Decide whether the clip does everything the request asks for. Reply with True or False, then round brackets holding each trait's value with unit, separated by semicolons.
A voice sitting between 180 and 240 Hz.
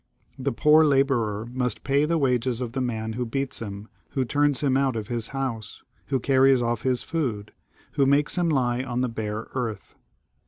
False (130 Hz)